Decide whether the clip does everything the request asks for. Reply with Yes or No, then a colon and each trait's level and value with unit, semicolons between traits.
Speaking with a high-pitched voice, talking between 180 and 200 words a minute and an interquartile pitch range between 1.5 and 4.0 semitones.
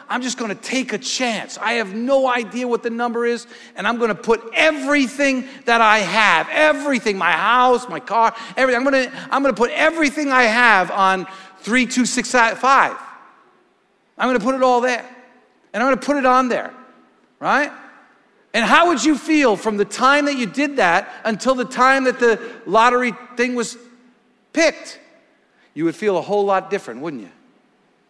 Yes: high, 245 Hz; average, 195 wpm; average, 2.8 semitones